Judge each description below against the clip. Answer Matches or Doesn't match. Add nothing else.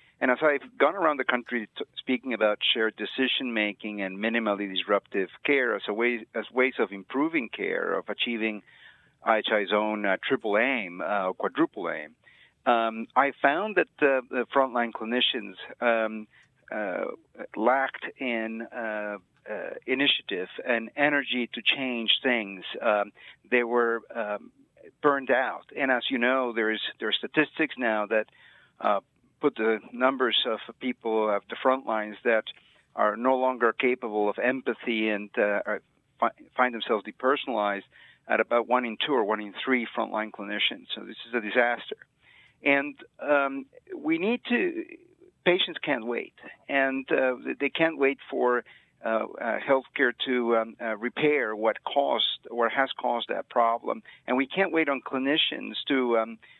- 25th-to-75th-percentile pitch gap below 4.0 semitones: Matches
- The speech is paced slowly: Doesn't match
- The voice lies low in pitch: Matches